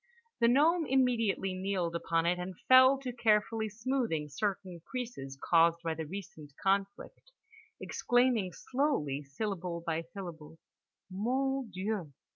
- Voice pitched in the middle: No, high, 195 Hz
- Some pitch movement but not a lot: No, wide, 6.5 semitones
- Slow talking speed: Yes, slow, 120 wpm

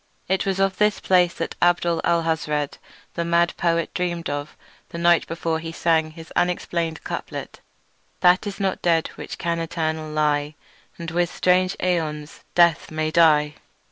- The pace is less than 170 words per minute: Yes, average, 155 wpm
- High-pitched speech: No, medium, 170 Hz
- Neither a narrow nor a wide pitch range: No, narrow, 1.8 semitones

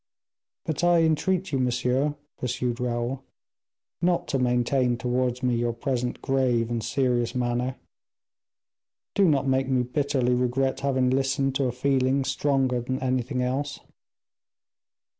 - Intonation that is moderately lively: No, narrow, 1.7 semitones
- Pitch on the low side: Yes, low, 130 Hz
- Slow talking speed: Yes, slow, 130 wpm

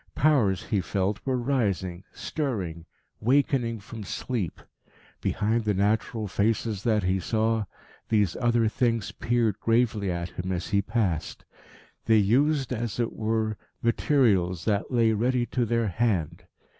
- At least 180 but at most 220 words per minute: No, slow, 135 wpm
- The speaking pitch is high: No, low, 110 Hz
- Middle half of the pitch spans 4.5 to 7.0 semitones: No, average, 3.3 semitones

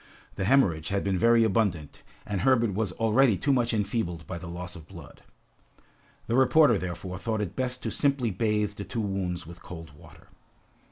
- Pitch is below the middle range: Yes, low, 100 Hz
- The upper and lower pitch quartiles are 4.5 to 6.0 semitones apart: Yes, average, 4.8 semitones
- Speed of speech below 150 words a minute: No, average, 180 wpm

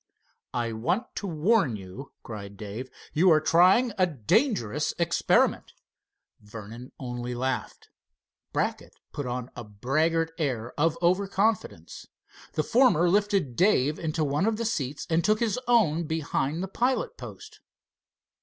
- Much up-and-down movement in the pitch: Yes, wide, 7.5 semitones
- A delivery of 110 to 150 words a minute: Yes, slow, 135 wpm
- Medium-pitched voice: Yes, medium, 155 Hz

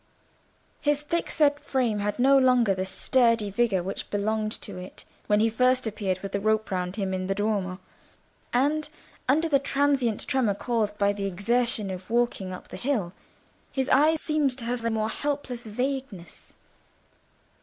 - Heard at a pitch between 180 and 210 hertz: No, high, 225 Hz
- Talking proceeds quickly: No, average, 165 wpm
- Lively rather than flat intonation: No, average, 4.7 semitones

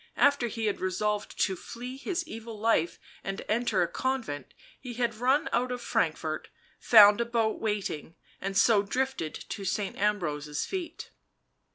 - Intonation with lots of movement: No, average, 4.1 semitones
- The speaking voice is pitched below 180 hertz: No, high, 220 Hz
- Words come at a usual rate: Yes, average, 160 wpm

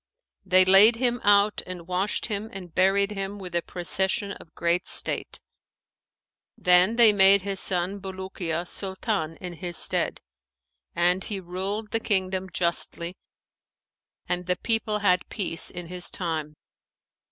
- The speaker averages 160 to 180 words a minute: No, average, 140 wpm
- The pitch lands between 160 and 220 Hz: Yes, high, 190 Hz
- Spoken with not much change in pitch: Yes, narrow, 2.2 semitones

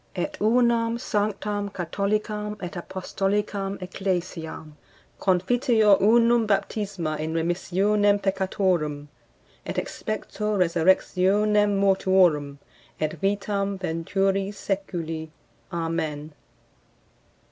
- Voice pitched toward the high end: Yes, high, 195 Hz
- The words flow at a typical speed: No, slow, 75 wpm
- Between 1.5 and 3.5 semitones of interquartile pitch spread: Yes, average, 3.1 semitones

